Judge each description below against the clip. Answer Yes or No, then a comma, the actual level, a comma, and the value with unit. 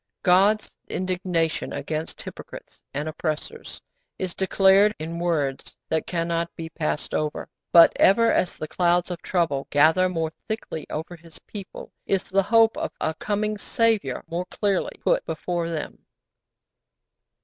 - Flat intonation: No, average, 3.2 semitones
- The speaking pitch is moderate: Yes, medium, 175 Hz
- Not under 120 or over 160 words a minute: Yes, average, 140 wpm